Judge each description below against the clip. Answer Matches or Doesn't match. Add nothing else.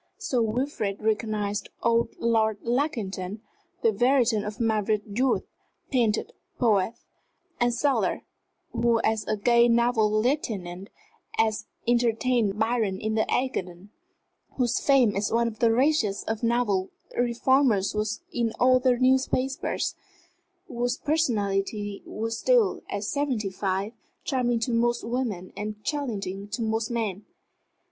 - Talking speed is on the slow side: Matches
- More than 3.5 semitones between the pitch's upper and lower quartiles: Doesn't match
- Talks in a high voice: Matches